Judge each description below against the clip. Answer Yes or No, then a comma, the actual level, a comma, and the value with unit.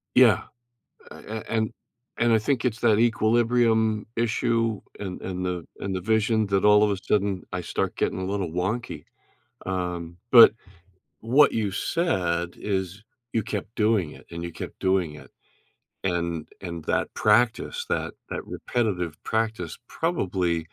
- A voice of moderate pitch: No, low, 105 Hz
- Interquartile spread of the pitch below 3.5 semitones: No, average, 4.0 semitones